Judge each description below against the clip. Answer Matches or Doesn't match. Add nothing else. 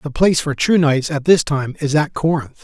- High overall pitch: Doesn't match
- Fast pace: Matches